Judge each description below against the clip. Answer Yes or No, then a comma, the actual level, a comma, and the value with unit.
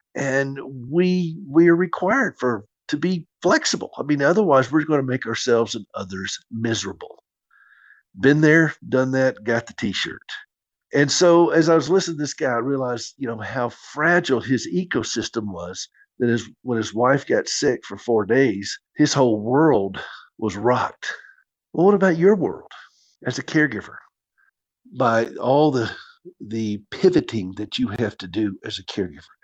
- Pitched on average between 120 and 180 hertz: Yes, low, 135 Hz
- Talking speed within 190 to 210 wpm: No, average, 165 wpm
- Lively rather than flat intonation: Yes, wide, 5.9 semitones